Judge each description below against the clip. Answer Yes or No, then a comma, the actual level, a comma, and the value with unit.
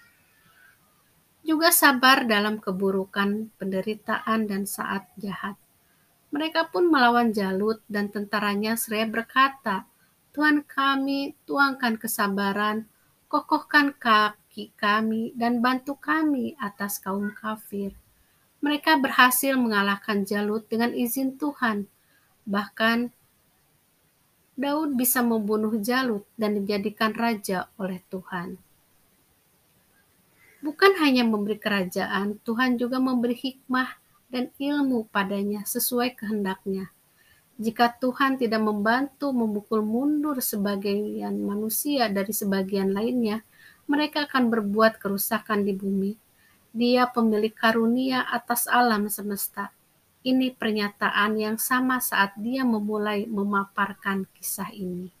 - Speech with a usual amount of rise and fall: Yes, average, 3.9 semitones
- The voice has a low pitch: No, high, 220 Hz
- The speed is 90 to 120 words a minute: Yes, average, 100 wpm